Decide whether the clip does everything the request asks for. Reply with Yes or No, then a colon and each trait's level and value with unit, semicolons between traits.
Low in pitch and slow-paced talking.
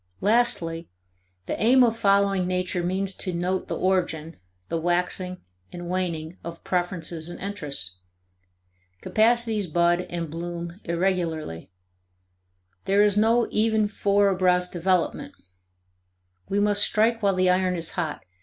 No: medium, 185 Hz; slow, 125 wpm